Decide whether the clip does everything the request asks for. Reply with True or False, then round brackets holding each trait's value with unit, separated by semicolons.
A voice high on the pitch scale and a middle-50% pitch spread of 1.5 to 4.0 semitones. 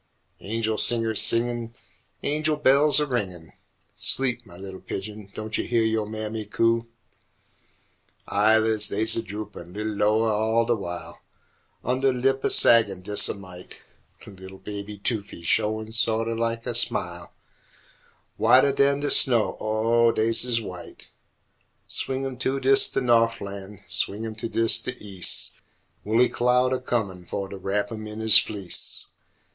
False (110 Hz; 2.6 semitones)